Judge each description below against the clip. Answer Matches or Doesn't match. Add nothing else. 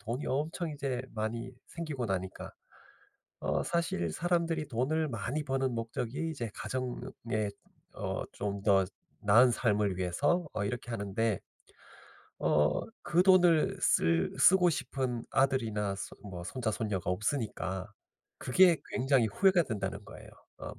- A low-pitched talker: Matches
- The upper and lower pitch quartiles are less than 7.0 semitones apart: Matches